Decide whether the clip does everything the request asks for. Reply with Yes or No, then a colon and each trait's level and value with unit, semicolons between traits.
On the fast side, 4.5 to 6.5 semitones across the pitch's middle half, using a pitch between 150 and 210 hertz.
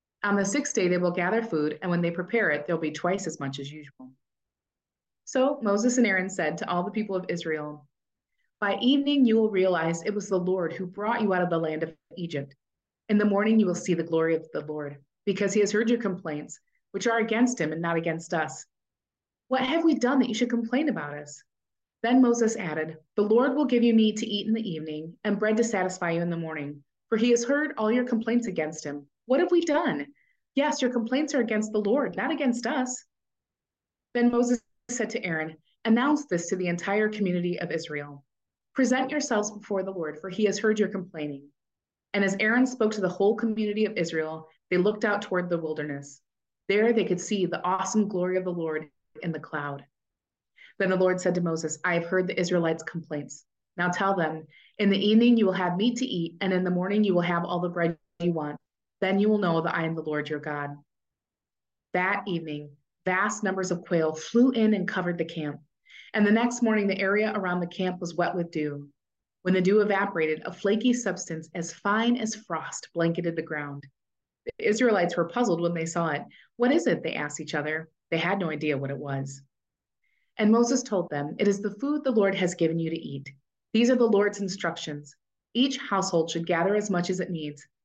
Yes: fast, 220 wpm; wide, 5.4 semitones; medium, 185 Hz